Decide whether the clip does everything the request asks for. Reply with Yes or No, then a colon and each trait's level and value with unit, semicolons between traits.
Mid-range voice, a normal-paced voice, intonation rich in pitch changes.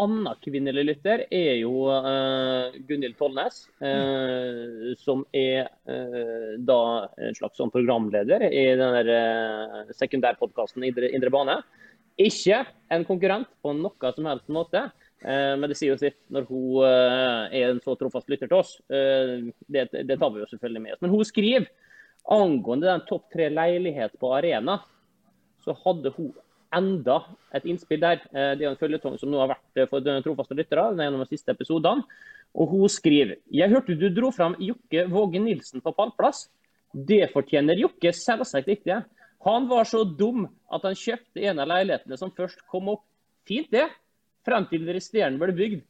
Yes: medium, 150 Hz; average, 175 wpm; wide, 7.3 semitones